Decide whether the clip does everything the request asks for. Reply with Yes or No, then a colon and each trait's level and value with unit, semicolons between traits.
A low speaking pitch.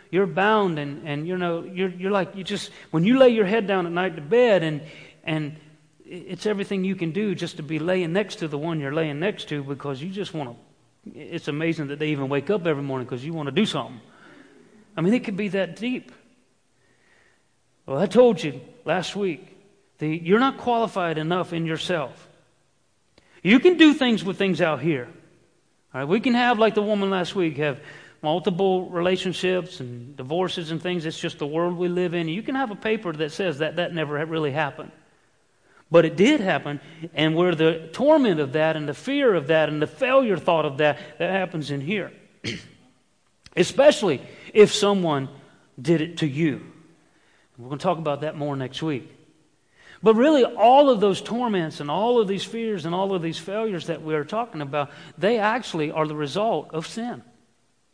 No: medium, 170 Hz